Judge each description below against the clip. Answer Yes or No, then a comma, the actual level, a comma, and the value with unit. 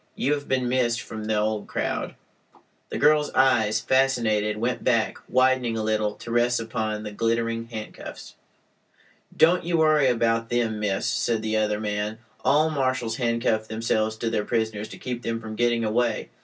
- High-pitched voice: No, low, 115 Hz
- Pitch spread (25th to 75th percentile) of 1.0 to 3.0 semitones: Yes, narrow, 2.4 semitones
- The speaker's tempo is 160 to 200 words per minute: Yes, average, 170 wpm